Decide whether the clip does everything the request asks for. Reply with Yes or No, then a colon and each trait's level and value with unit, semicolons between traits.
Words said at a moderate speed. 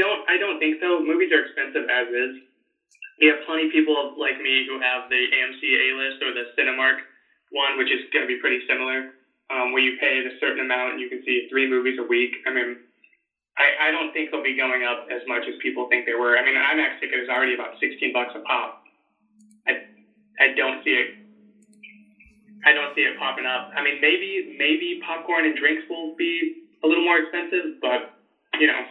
No: fast, 215 wpm